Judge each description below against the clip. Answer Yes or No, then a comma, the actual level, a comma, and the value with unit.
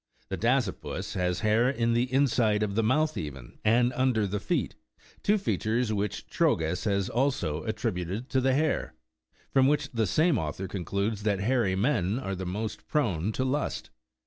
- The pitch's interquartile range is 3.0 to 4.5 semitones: No, average, 5.1 semitones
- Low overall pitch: Yes, low, 110 Hz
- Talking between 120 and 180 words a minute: Yes, average, 170 wpm